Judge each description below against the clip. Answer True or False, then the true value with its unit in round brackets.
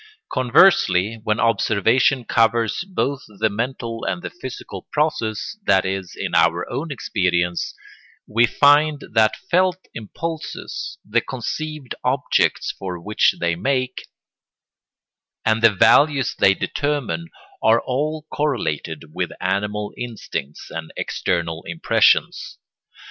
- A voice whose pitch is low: True (115 Hz)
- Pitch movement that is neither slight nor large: False (6.3 semitones)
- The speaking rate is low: True (110 wpm)